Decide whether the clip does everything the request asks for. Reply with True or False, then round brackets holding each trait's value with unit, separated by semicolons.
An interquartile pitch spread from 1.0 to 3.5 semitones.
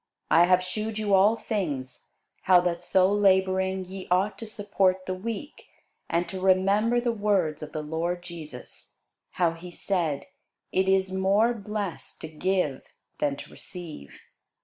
True (2.8 semitones)